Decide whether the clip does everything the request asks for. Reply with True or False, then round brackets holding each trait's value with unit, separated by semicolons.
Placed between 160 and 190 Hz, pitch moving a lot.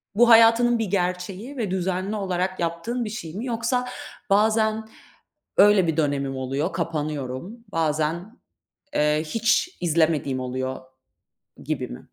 True (185 Hz; 6.3 semitones)